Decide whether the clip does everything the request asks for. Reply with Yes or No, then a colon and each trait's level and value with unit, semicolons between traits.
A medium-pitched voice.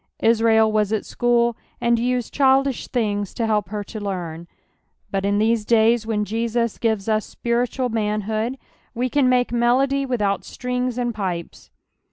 No: high, 230 Hz